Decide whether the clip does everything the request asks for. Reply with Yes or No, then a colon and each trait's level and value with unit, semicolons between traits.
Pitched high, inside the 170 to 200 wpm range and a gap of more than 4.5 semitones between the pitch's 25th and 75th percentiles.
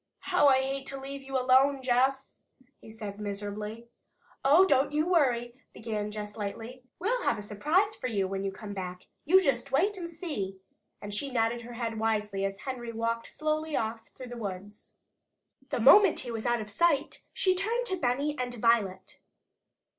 Yes: high, 245 Hz; average, 180 wpm; average, 5.2 semitones